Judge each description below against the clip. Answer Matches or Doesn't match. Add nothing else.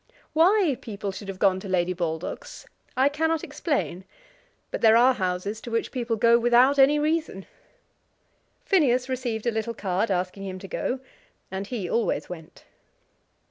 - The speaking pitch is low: Doesn't match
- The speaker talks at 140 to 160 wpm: Matches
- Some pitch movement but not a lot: Doesn't match